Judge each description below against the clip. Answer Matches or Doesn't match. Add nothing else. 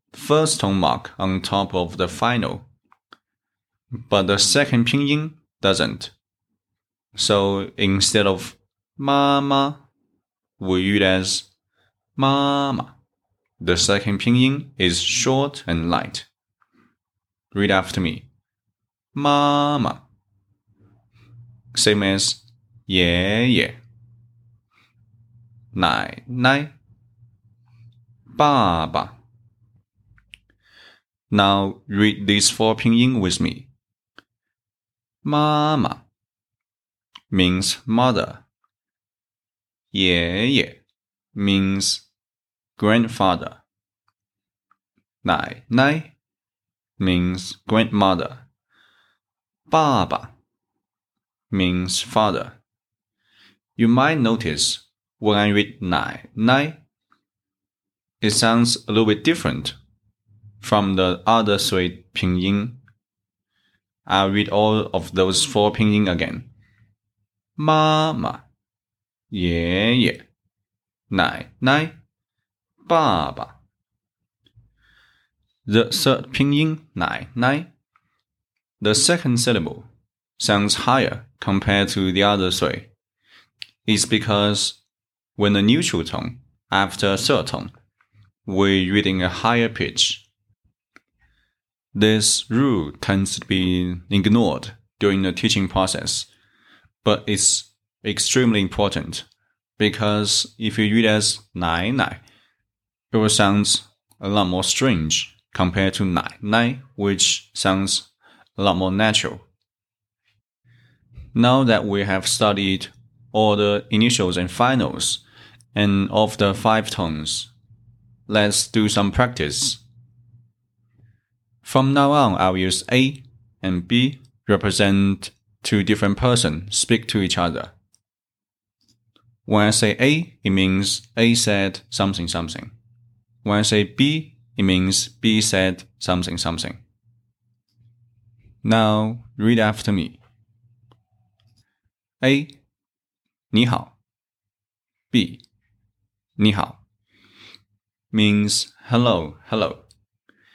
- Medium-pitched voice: Doesn't match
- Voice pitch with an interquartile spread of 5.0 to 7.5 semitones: Doesn't match